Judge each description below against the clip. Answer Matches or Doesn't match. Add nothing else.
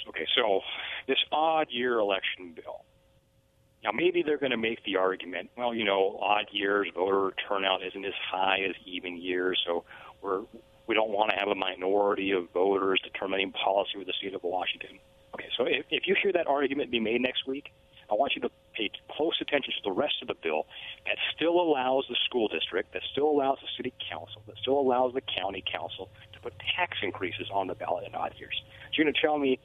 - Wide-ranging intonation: Matches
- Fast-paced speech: Matches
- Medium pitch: Doesn't match